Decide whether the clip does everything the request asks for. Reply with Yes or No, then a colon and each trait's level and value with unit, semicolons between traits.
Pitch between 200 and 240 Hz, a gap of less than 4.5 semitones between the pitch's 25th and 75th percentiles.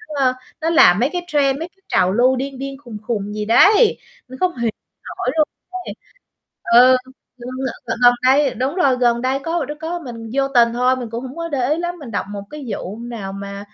No: very high, 260 Hz; average, 4.1 semitones